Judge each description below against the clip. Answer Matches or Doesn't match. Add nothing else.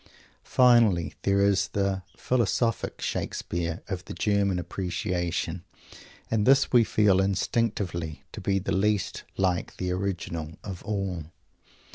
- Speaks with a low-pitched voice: Matches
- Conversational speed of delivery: Doesn't match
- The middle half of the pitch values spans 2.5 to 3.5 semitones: Matches